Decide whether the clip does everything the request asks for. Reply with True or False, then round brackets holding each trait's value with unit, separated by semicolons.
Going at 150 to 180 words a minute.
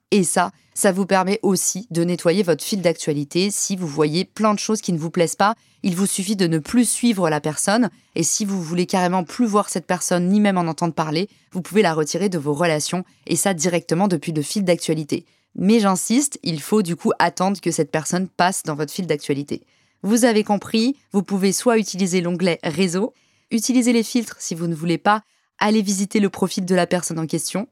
False (215 wpm)